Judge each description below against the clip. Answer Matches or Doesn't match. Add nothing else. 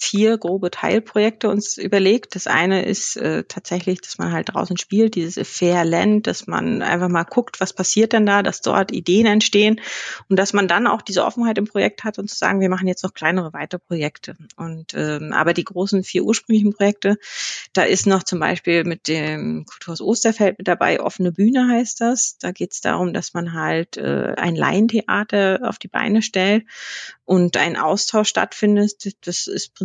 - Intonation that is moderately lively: Matches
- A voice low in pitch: Doesn't match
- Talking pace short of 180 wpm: Doesn't match